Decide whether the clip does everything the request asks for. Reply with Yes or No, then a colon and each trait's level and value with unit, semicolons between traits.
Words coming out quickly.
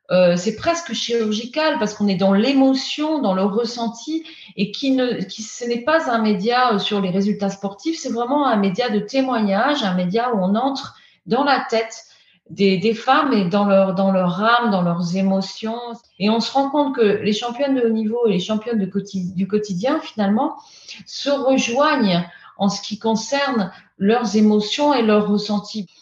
No: average, 185 wpm